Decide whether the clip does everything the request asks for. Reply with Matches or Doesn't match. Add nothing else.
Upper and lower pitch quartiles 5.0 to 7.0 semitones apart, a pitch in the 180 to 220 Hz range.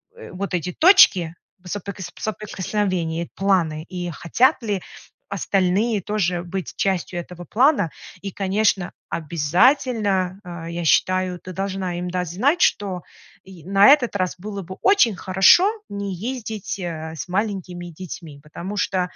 Doesn't match